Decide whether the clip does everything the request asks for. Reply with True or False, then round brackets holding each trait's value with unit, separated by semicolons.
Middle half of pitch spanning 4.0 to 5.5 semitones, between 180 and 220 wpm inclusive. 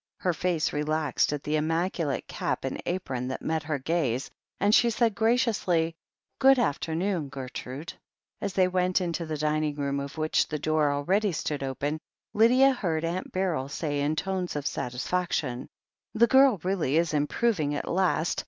False (4.3 semitones; 170 wpm)